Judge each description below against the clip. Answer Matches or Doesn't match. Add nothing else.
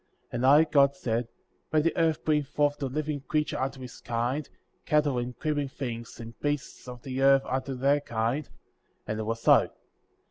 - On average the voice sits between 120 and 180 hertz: Matches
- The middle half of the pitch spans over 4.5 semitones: Doesn't match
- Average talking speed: Matches